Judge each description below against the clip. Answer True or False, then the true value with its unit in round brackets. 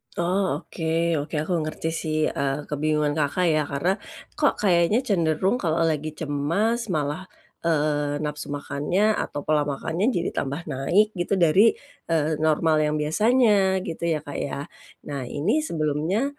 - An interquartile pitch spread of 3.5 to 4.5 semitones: True (3.8 semitones)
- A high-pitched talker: False (160 Hz)